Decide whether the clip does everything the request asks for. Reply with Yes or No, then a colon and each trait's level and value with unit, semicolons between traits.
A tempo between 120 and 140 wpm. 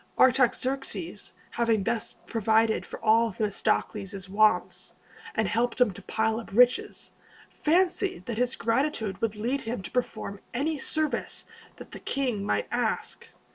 Yes: slow, 135 wpm